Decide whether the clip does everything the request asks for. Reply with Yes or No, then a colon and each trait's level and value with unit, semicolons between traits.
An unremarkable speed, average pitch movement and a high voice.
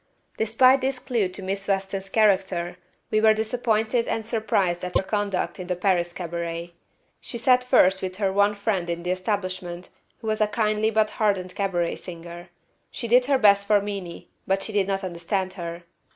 Yes: average, 180 wpm; average, 3.2 semitones; high, 195 Hz